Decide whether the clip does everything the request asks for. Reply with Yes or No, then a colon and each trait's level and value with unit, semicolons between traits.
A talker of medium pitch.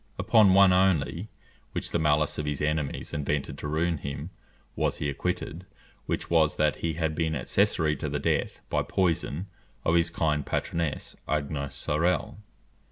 No: very low, 80 Hz